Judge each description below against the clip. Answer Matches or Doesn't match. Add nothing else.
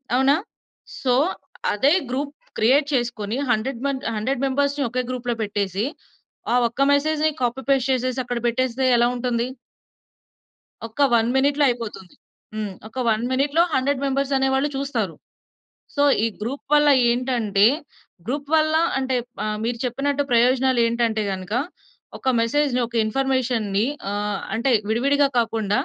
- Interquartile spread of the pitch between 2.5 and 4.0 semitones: Matches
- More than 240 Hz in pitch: Matches